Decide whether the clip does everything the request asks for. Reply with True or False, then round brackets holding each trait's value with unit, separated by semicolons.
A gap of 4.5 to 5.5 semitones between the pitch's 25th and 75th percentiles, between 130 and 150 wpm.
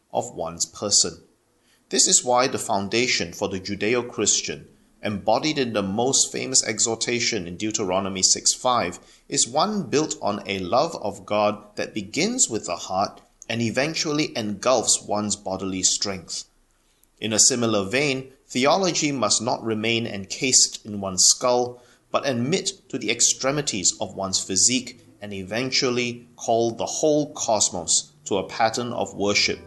False (3.9 semitones; 145 wpm)